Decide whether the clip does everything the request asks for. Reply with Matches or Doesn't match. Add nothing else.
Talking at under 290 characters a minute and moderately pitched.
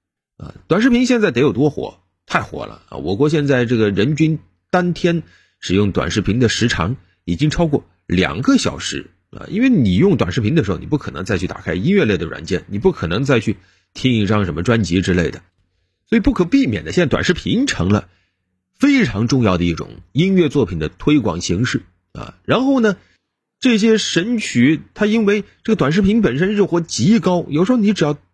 Doesn't match